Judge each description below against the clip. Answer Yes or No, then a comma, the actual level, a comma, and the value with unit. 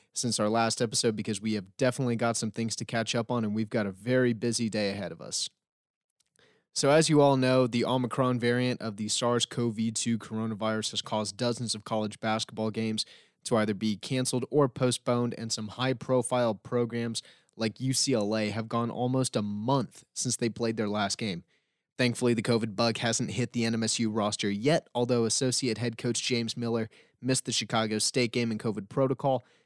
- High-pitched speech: No, low, 115 Hz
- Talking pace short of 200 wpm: Yes, average, 190 wpm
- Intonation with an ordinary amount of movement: No, narrow, 2.2 semitones